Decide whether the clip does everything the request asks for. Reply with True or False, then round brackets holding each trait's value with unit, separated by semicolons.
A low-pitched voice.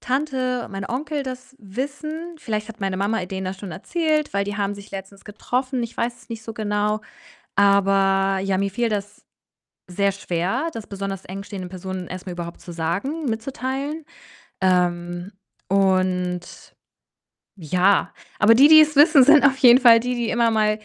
False (205 Hz)